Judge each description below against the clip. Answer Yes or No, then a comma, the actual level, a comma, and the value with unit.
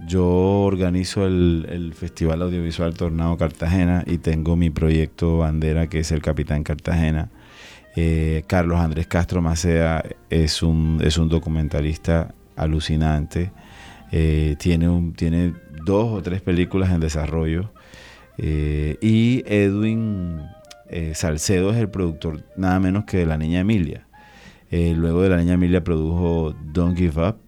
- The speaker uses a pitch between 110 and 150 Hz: No, very low, 85 Hz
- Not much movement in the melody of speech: Yes, narrow, 2.3 semitones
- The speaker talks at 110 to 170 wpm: Yes, average, 140 wpm